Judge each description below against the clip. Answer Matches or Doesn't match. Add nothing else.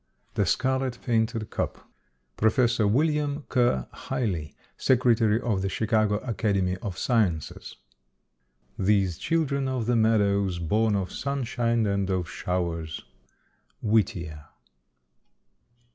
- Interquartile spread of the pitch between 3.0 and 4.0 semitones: Doesn't match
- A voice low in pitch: Matches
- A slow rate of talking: Matches